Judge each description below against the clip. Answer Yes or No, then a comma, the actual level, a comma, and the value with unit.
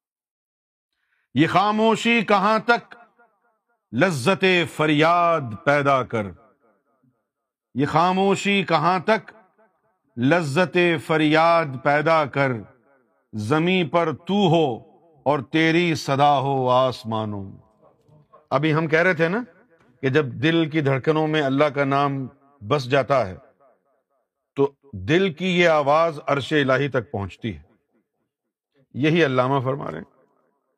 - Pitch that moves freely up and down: No, average, 4.4 semitones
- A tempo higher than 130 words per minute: No, average, 115 wpm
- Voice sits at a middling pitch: Yes, medium, 150 Hz